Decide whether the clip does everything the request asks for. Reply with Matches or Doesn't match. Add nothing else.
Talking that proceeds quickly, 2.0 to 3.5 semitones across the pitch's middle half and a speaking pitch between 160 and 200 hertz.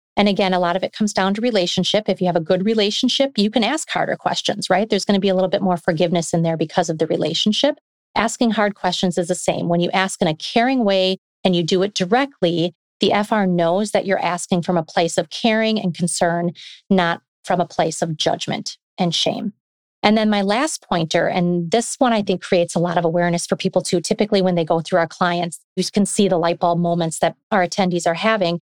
Matches